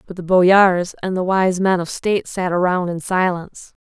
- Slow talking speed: No, fast, 205 wpm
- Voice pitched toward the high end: No, medium, 180 Hz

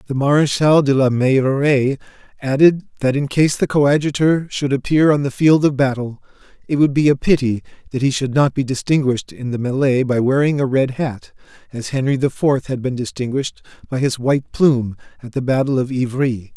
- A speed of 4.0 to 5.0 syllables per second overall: No, 5.4 syllables/s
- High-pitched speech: No, low, 135 Hz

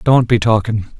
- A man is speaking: Yes, male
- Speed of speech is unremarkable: Yes, average, 180 wpm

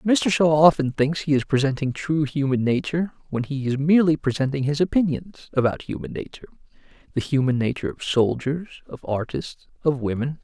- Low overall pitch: No, medium, 145 Hz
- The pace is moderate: Yes, average, 160 wpm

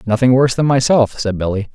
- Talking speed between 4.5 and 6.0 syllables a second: No, 6.3 syllables/s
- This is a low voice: Yes, low, 120 Hz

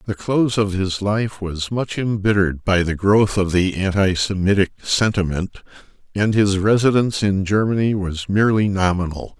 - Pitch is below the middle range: Yes, low, 100 Hz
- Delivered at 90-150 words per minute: Yes, average, 145 wpm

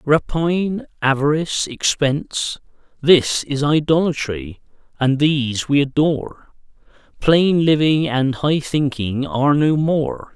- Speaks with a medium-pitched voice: Yes, medium, 145 Hz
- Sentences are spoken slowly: Yes, slow, 105 wpm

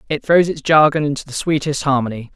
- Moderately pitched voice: Yes, medium, 145 Hz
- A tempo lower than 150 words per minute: No, fast, 205 wpm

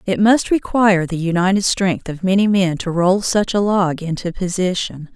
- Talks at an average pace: Yes, average, 185 wpm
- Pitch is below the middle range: No, medium, 185 Hz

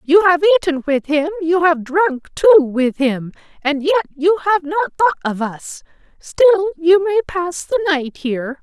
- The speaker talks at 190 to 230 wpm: No, average, 180 wpm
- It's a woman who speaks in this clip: Yes, female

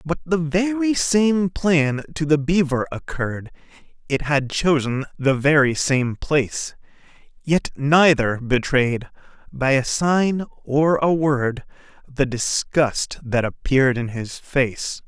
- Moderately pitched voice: Yes, medium, 145 Hz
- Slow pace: Yes, slow, 125 wpm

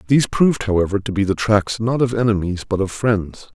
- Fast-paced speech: Yes, fast, 220 wpm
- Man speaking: Yes, male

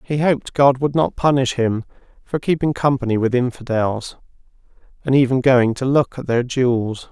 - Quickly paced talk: No, average, 170 wpm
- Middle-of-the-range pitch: No, low, 130 Hz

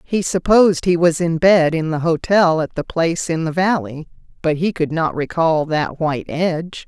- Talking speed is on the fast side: No, average, 190 wpm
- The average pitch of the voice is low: No, medium, 165 Hz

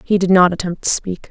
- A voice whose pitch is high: No, medium, 180 Hz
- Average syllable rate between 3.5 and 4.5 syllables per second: No, 5.8 syllables/s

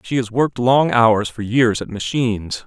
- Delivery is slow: No, average, 200 wpm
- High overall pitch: No, low, 115 Hz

